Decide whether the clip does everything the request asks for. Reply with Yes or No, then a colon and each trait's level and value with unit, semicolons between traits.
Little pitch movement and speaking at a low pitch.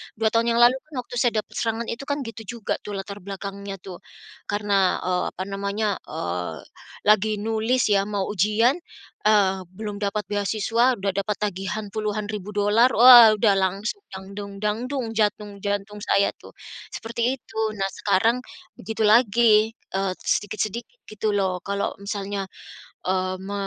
No: narrow, 2.2 semitones; high, 210 Hz